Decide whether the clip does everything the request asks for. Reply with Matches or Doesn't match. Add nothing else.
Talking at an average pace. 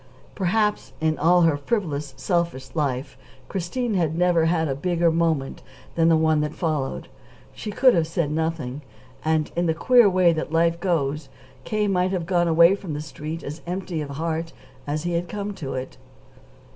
Matches